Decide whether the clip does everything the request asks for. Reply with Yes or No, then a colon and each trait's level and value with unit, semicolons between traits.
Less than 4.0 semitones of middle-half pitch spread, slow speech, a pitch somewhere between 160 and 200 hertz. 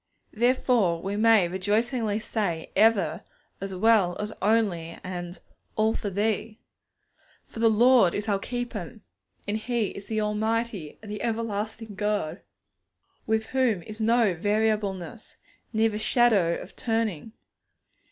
No: narrow, 2.6 semitones; slow, 125 wpm; high, 215 Hz